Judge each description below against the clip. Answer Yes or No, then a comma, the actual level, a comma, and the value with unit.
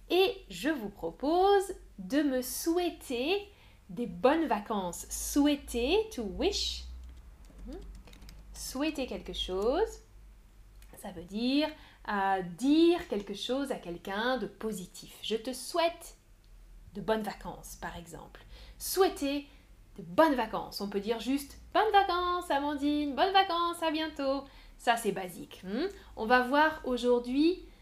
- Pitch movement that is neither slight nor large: No, wide, 8.2 semitones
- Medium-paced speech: No, slow, 125 wpm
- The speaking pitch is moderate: No, very high, 260 Hz